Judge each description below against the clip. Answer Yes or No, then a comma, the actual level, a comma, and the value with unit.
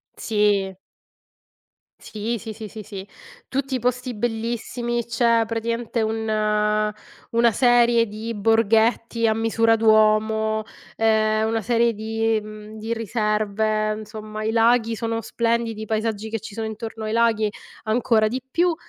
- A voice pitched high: Yes, high, 225 Hz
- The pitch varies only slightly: Yes, narrow, 1.3 semitones